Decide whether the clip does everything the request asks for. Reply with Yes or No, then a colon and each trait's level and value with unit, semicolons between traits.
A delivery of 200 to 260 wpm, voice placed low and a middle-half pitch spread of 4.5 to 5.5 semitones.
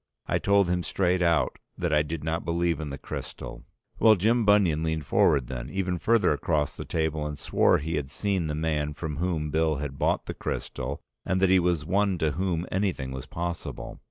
No: fast, 205 wpm; very low, 80 Hz; average, 3.5 semitones